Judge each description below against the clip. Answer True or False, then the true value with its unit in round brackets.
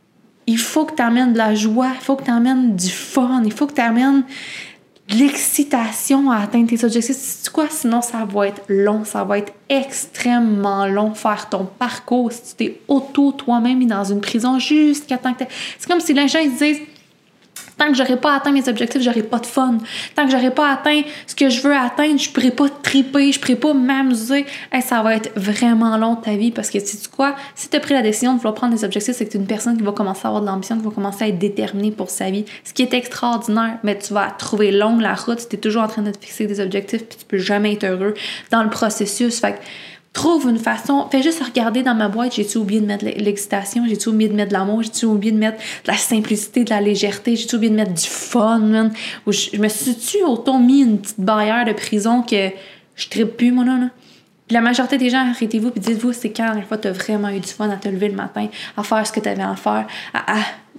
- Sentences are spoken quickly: True (260 wpm)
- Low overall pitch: False (230 Hz)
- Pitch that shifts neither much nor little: True (3.6 semitones)